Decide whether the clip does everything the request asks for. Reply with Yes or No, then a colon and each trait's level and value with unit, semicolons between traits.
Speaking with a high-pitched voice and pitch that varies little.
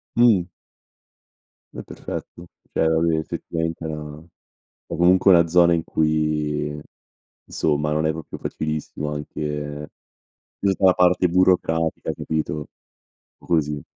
No: very low, 80 Hz; narrow, 2.3 semitones